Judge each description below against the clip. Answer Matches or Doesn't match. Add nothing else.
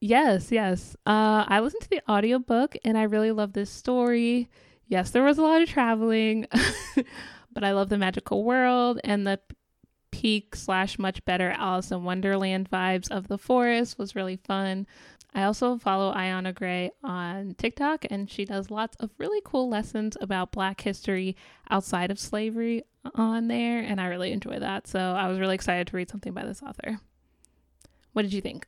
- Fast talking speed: Doesn't match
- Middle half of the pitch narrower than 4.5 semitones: Matches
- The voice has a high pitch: Matches